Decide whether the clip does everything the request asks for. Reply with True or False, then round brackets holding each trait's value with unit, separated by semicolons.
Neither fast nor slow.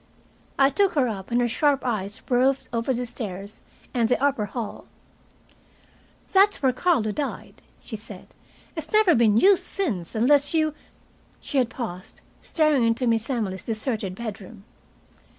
True (150 wpm)